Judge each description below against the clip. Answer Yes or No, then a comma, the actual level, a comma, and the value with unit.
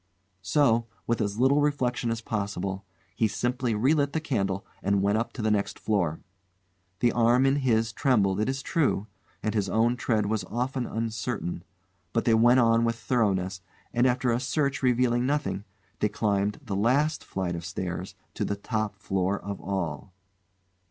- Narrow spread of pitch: No, average, 3.8 semitones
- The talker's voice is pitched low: Yes, low, 115 Hz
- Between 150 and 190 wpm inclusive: Yes, average, 170 wpm